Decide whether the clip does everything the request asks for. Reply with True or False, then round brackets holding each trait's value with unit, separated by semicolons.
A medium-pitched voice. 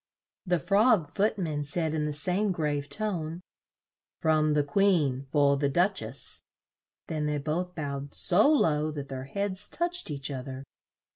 True (155 Hz)